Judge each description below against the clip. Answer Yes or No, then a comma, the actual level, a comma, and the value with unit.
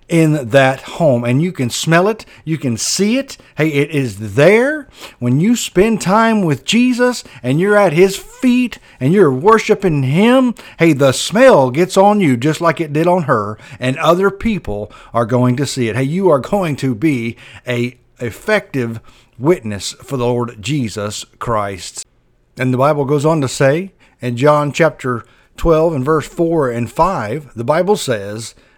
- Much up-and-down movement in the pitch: Yes, wide, 6.8 semitones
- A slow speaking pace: No, average, 175 wpm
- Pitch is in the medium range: Yes, medium, 145 Hz